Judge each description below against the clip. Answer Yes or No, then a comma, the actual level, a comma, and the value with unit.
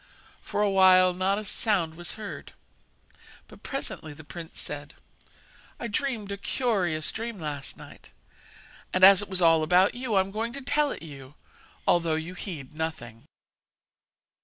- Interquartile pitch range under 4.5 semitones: No, average, 4.8 semitones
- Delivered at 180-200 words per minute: No, average, 160 wpm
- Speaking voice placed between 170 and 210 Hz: Yes, medium, 185 Hz